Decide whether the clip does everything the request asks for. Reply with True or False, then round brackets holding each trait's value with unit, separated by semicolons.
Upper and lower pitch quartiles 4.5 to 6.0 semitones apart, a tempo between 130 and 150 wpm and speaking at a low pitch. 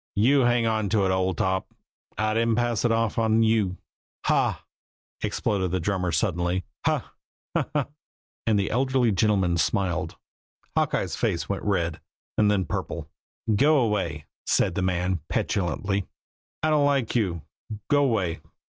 False (3.9 semitones; 145 wpm; 105 Hz)